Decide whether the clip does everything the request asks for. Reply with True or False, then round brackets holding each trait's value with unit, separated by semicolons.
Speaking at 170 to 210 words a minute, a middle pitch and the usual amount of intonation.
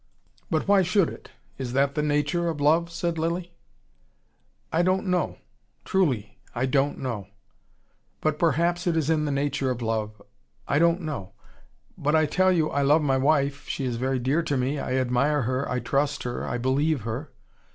True (185 wpm; 145 Hz; 4.0 semitones)